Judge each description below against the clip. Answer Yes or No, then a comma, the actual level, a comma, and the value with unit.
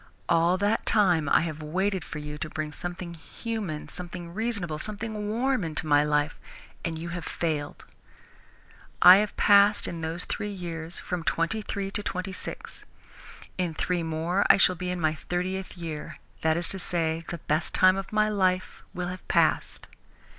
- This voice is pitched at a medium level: Yes, medium, 175 Hz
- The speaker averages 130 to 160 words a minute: No, average, 175 wpm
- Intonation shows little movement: No, average, 3.3 semitones